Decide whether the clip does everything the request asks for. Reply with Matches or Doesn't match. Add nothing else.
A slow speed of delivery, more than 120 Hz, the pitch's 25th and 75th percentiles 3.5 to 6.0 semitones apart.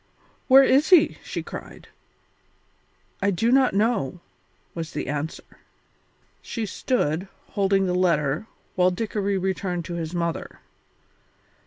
Matches